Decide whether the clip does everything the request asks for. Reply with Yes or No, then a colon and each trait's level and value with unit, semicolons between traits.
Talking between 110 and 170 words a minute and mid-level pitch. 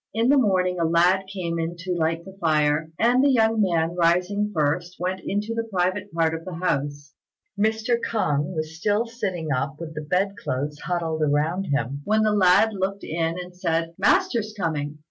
No: average, 185 wpm; medium, 175 Hz